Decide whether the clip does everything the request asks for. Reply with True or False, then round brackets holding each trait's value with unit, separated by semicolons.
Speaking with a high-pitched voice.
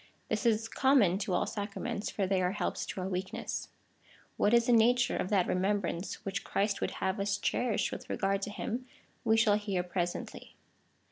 True (205 Hz)